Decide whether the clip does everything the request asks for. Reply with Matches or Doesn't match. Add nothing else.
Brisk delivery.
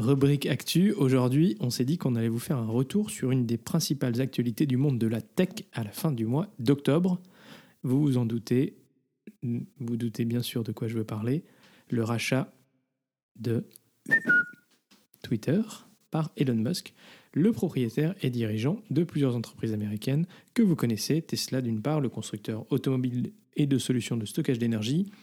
Doesn't match